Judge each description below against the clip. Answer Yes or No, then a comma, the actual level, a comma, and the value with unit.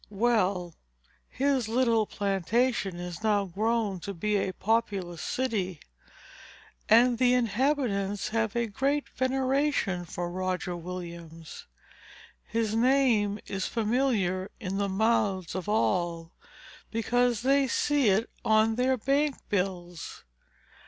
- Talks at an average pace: No, slow, 110 wpm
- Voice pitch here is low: No, high, 215 Hz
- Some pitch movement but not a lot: Yes, average, 4.8 semitones